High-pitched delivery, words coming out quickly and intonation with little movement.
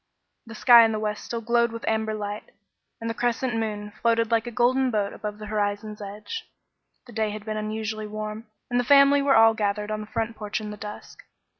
Yes: high, 220 Hz; fast, 215 wpm; narrow, 1.6 semitones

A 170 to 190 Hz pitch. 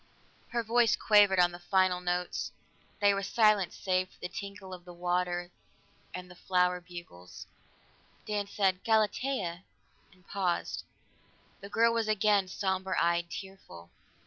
Yes: medium, 185 Hz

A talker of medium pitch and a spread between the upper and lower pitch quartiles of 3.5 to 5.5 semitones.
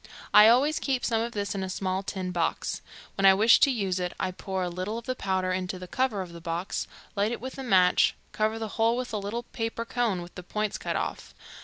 No: high, 200 Hz; average, 3.9 semitones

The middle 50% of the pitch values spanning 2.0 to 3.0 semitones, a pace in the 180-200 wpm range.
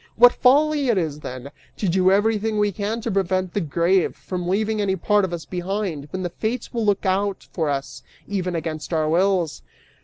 No: average, 3.6 semitones; average, 195 wpm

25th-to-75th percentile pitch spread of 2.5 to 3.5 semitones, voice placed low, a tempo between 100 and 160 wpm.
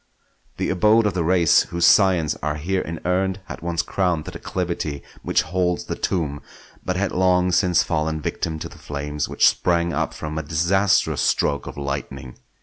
No: average, 3.0 semitones; very low, 85 Hz; average, 175 wpm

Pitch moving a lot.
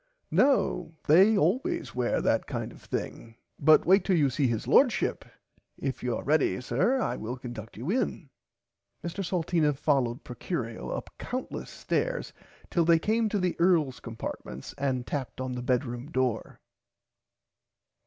Yes: wide, 6.8 semitones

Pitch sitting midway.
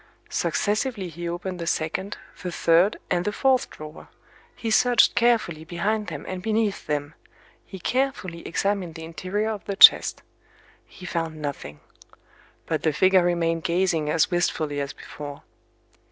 Yes: medium, 175 Hz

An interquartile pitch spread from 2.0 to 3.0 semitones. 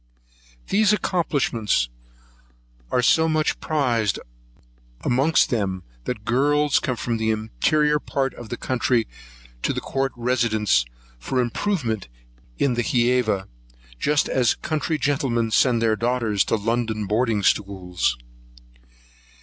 No: average, 4.1 semitones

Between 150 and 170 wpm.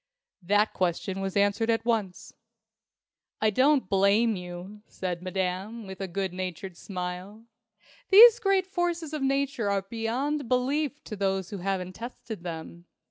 No: average, 140 wpm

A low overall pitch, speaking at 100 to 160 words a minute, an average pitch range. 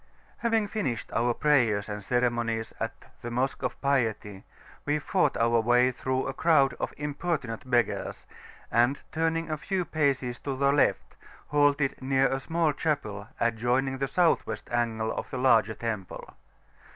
Yes: low, 130 Hz; average, 155 wpm; average, 3.8 semitones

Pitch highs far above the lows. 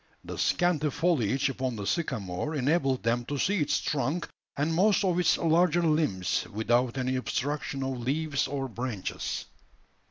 No: average, 4.5 semitones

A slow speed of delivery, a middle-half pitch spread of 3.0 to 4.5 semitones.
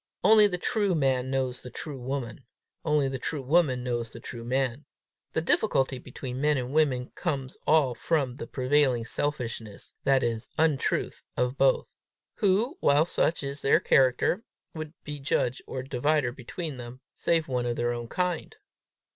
No: average, 165 wpm; average, 3.7 semitones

